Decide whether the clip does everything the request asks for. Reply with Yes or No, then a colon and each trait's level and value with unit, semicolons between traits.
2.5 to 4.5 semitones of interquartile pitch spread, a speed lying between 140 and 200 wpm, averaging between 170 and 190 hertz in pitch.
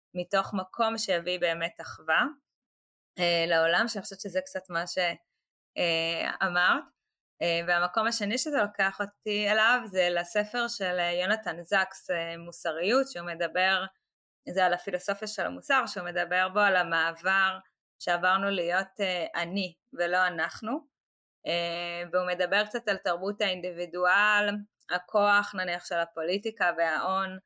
No: average, 2.8 semitones; average, 125 wpm; medium, 185 Hz